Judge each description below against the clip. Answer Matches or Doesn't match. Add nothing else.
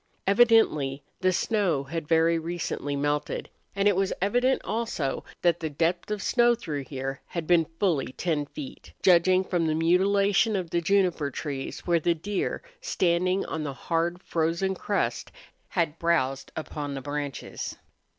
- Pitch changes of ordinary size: Matches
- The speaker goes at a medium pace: Matches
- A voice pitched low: Doesn't match